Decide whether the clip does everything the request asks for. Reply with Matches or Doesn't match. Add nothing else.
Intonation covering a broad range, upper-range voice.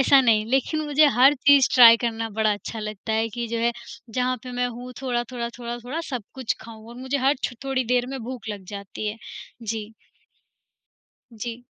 Doesn't match